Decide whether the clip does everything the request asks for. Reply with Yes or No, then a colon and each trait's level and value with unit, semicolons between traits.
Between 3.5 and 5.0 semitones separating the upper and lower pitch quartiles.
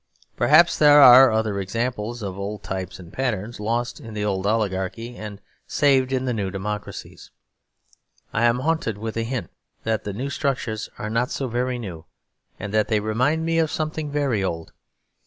Yes: average, 4.1 semitones